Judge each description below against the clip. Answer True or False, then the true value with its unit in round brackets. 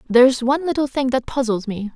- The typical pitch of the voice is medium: False (250 Hz)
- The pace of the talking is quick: True (245 wpm)